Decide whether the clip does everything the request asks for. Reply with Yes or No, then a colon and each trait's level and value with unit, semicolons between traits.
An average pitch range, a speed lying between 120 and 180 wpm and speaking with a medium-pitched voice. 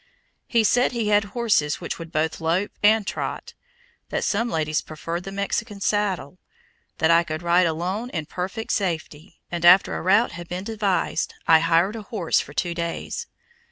Yes: average, 3.8 semitones; average, 175 wpm; medium, 180 Hz